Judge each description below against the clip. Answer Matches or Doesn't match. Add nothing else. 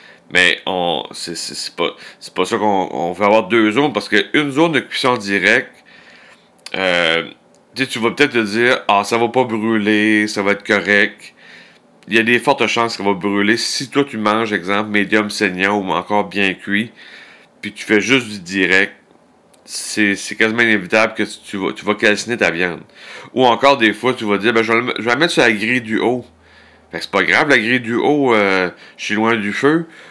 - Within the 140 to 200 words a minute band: Doesn't match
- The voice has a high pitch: Doesn't match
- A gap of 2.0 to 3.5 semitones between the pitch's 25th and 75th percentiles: Matches